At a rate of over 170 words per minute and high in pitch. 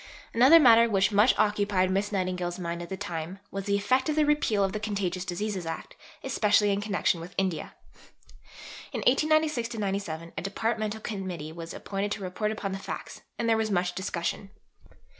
Yes: average, 180 wpm; high, 200 Hz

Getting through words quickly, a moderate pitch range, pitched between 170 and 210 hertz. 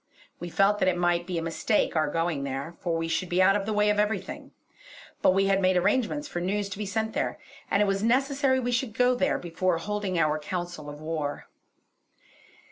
Yes: fast, 215 wpm; average, 3.9 semitones; medium, 185 Hz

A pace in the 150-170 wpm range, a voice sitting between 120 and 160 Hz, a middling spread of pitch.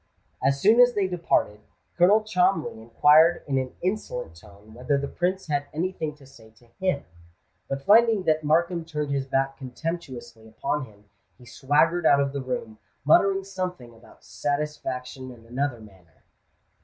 No: average, 165 wpm; medium, 140 Hz; wide, 5.8 semitones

